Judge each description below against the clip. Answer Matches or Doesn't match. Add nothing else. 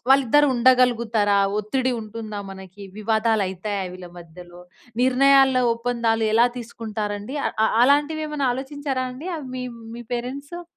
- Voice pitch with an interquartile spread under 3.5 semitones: Doesn't match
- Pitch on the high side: Matches